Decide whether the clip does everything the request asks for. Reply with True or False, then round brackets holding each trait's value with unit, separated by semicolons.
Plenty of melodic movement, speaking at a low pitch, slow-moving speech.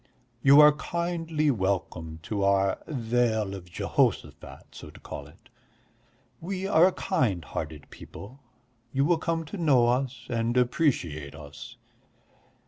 True (8.0 semitones; 120 Hz; 130 wpm)